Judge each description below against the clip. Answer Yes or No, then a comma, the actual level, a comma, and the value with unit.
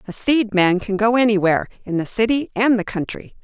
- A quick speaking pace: Yes, fast, 210 wpm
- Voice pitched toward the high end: Yes, high, 215 Hz